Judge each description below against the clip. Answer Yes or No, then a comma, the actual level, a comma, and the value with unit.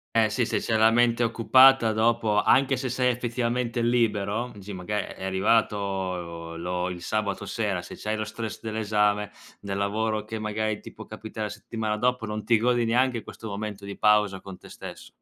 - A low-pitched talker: Yes, low, 110 Hz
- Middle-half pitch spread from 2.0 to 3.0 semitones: Yes, narrow, 2.4 semitones